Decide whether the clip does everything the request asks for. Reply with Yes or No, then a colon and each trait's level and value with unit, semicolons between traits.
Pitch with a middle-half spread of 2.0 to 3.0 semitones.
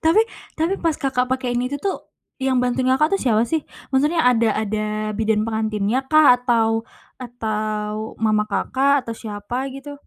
No: average, 4.1 semitones